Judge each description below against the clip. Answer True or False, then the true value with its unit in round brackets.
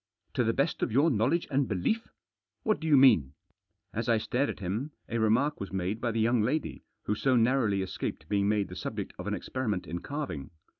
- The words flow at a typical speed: False (230 wpm)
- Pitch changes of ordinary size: True (5.0 semitones)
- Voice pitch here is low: True (115 Hz)